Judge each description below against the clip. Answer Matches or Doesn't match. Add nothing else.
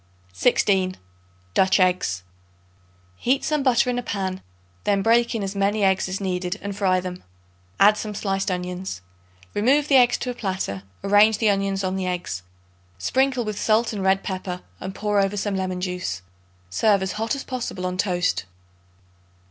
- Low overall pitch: Doesn't match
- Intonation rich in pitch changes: Doesn't match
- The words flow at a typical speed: Matches